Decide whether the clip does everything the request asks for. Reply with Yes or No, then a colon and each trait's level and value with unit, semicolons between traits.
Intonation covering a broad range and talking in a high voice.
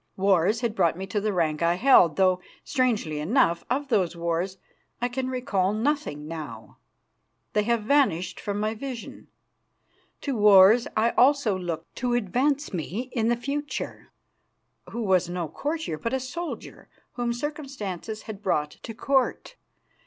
Yes: wide, 6.0 semitones; high, 215 Hz